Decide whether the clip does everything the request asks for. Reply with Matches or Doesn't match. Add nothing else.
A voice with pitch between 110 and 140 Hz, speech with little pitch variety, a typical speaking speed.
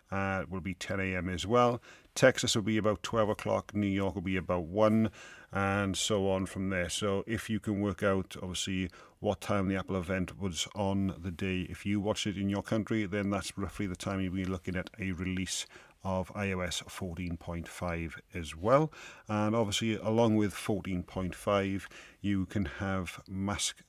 Doesn't match